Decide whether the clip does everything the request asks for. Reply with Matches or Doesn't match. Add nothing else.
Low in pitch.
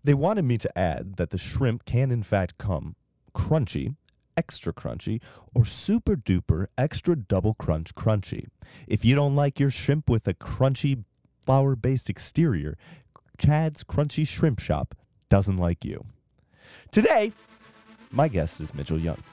Matches